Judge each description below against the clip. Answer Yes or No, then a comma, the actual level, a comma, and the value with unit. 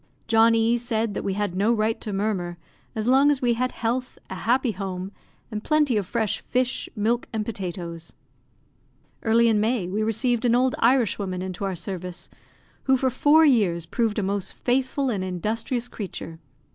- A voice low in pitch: No, high, 220 Hz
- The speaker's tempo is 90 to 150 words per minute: No, average, 175 wpm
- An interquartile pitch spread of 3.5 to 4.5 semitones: Yes, average, 4.0 semitones